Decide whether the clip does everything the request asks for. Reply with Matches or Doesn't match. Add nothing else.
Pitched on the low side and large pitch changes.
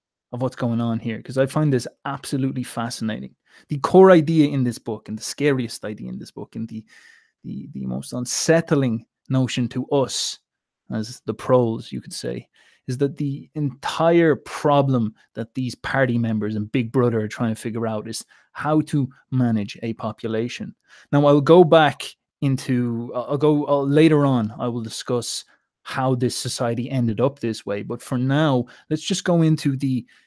Doesn't match